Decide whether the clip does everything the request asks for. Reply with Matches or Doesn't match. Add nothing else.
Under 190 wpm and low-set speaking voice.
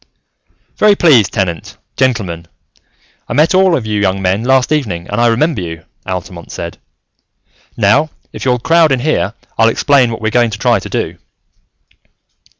Matches